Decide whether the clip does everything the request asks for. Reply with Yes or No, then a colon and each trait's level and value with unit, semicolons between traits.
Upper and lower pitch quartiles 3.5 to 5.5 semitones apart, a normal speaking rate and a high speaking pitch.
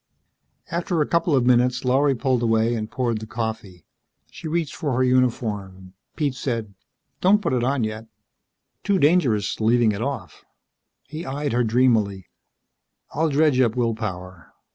No: average, 4.3 semitones; average, 155 wpm; low, 125 Hz